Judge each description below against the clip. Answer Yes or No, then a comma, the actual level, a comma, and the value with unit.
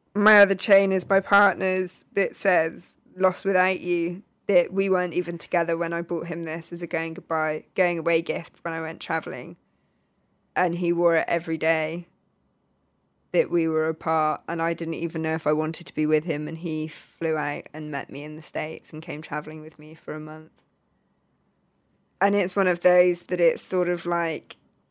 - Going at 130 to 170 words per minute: No, average, 200 wpm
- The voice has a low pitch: No, medium, 170 Hz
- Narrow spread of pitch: Yes, narrow, 2.3 semitones